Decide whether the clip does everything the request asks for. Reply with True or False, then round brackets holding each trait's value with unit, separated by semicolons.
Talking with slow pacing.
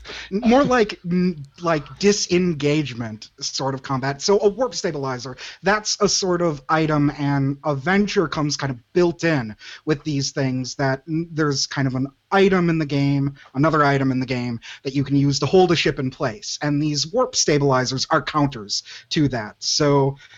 False (175 wpm)